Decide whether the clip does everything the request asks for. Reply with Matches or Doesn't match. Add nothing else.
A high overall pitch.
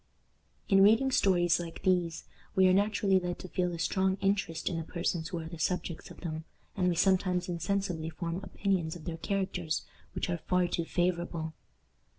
Doesn't match